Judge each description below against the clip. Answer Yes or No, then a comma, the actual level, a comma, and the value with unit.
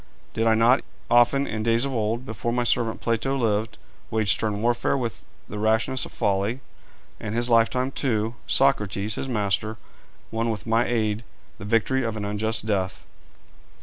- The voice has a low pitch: Yes, low, 115 Hz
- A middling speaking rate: Yes, average, 165 wpm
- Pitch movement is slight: Yes, narrow, 2.2 semitones